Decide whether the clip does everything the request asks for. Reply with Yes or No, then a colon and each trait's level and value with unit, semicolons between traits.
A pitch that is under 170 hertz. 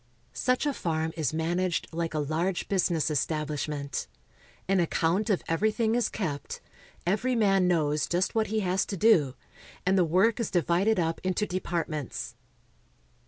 No: medium, 175 Hz